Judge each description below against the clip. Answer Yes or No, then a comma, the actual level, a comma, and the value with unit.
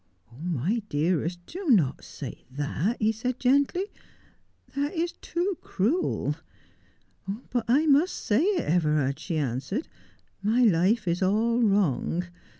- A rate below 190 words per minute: Yes, average, 140 wpm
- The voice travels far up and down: Yes, wide, 7.9 semitones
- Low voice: No, high, 210 Hz